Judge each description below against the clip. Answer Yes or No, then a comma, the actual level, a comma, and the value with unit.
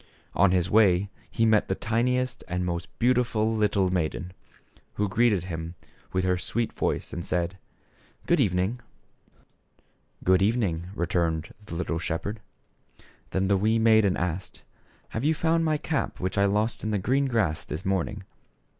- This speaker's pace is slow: No, average, 165 wpm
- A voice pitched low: Yes, low, 100 Hz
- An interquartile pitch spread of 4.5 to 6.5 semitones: No, average, 3.9 semitones